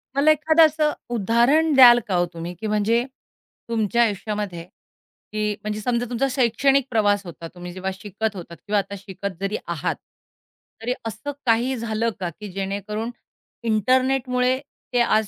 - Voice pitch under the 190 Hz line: No, high, 220 Hz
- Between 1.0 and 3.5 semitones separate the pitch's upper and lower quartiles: No, average, 3.9 semitones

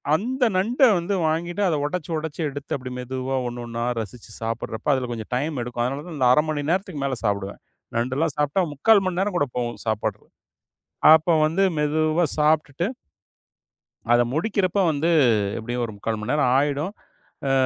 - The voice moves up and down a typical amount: No, wide, 5.7 semitones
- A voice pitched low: No, medium, 145 Hz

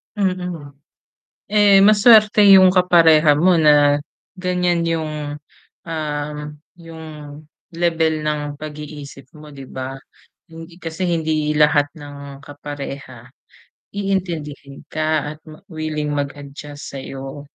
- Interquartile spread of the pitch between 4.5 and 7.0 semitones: No, average, 2.9 semitones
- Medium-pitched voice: Yes, medium, 155 Hz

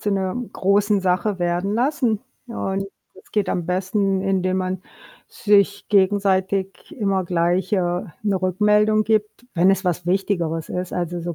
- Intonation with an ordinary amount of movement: No, narrow, 2.1 semitones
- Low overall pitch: No, high, 190 Hz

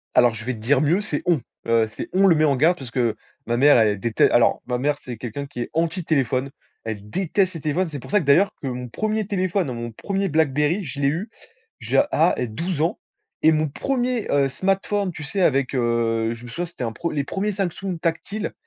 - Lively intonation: Yes, wide, 6.9 semitones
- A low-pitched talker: No, medium, 150 Hz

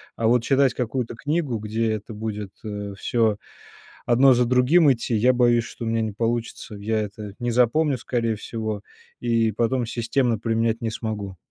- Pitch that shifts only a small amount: Yes, narrow, 2.1 semitones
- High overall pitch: No, low, 115 Hz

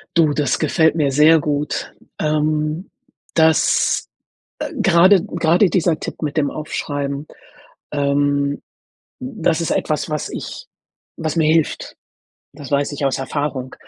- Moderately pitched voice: Yes, medium, 150 Hz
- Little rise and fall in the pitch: Yes, narrow, 2.1 semitones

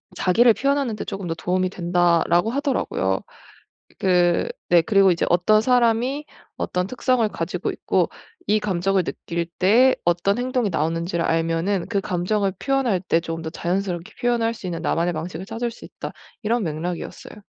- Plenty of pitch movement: No, average, 4.9 semitones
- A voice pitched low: No, medium, 185 Hz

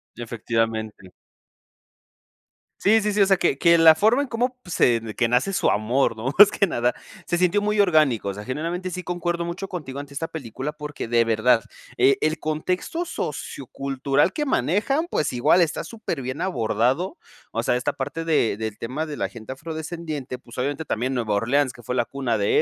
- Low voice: No, medium, 145 Hz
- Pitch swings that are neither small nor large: No, wide, 6.3 semitones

